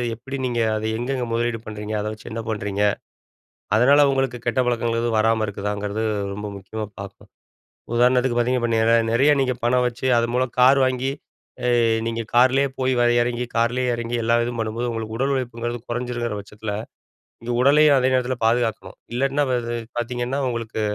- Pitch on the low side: Yes, low, 120 Hz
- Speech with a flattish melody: Yes, narrow, 2.1 semitones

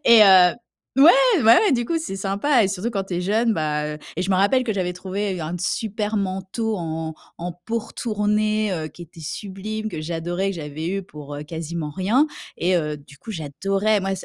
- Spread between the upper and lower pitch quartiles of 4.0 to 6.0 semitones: Yes, average, 4.5 semitones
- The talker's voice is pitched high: Yes, high, 195 Hz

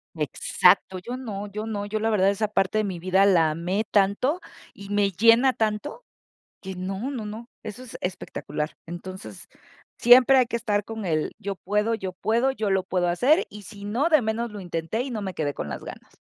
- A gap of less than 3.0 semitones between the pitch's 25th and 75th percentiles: No, average, 3.5 semitones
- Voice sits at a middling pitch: No, high, 205 Hz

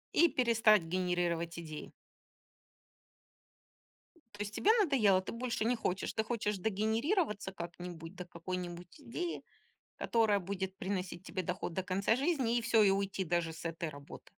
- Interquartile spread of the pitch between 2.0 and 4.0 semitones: No, average, 4.4 semitones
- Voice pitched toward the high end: Yes, high, 195 Hz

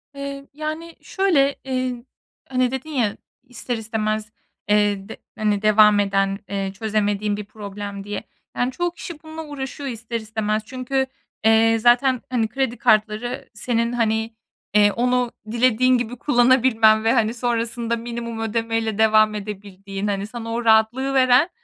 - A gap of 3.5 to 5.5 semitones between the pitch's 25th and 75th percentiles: No, average, 3.1 semitones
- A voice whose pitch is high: Yes, high, 230 Hz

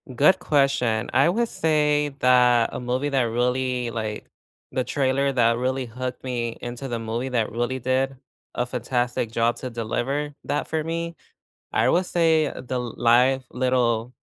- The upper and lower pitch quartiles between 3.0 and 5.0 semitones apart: No, narrow, 2.5 semitones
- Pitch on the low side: Yes, low, 125 Hz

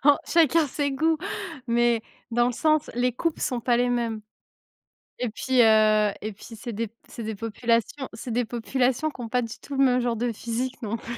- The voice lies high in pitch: Yes, high, 240 Hz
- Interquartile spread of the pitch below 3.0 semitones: Yes, narrow, 2.4 semitones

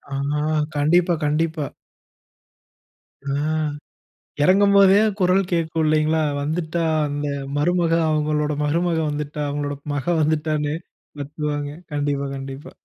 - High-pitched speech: No, medium, 150 Hz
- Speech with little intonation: Yes, narrow, 2.3 semitones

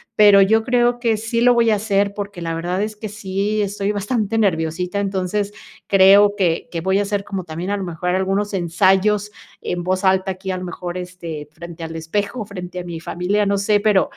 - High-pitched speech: Yes, high, 195 Hz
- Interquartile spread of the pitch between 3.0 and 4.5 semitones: No, narrow, 2.6 semitones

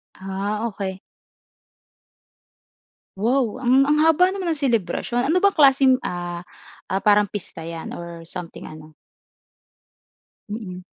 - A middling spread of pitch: No, wide, 7.0 semitones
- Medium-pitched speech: No, high, 210 Hz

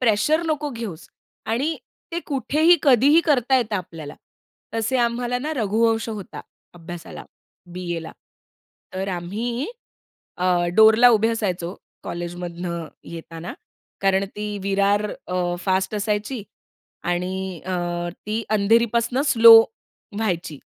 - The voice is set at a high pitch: Yes, high, 210 Hz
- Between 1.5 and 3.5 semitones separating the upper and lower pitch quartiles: No, average, 4.7 semitones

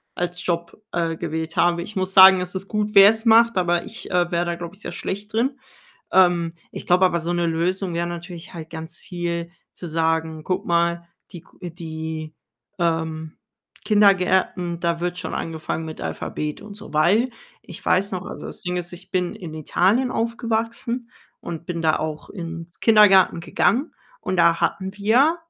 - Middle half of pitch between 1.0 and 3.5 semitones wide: Yes, average, 2.8 semitones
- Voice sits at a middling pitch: Yes, medium, 175 Hz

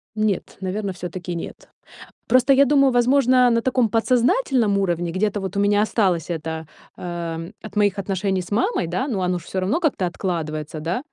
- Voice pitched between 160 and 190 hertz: No, high, 200 Hz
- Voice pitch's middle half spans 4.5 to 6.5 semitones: Yes, wide, 5.4 semitones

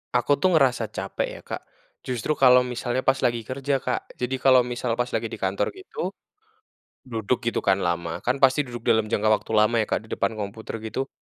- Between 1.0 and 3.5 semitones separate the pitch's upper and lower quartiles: Yes, average, 2.9 semitones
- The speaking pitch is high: No, low, 120 Hz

